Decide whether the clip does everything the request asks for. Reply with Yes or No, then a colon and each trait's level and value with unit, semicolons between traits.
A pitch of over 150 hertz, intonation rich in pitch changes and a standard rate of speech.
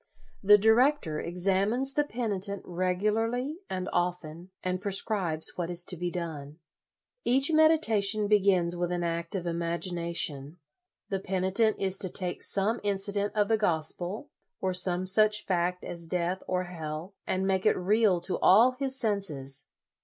No: medium, 185 Hz; average, 3.2 semitones; average, 155 wpm